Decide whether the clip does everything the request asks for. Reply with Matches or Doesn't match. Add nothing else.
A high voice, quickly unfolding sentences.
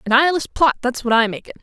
Matches